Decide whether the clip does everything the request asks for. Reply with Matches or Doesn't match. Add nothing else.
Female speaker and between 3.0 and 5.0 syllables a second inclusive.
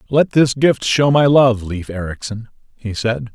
Doesn't match